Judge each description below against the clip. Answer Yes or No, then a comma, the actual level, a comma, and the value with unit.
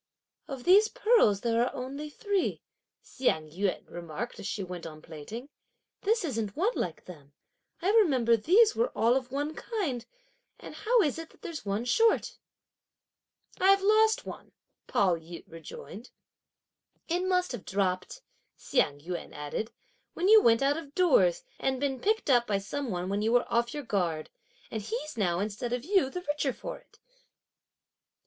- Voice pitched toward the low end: No, very high, 250 Hz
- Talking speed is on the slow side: No, average, 165 wpm